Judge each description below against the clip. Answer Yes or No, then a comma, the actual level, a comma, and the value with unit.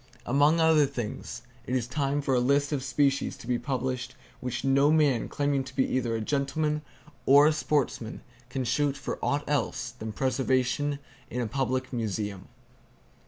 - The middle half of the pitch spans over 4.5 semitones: No, narrow, 2.6 semitones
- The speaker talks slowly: No, average, 165 wpm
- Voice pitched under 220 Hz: Yes, low, 135 Hz